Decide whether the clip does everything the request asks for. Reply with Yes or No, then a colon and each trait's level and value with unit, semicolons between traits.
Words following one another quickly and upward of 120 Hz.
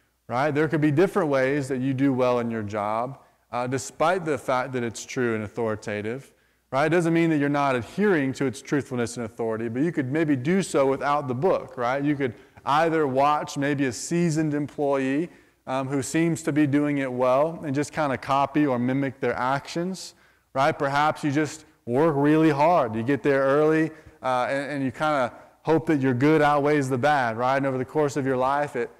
Yes: fast, 215 wpm; medium, 140 Hz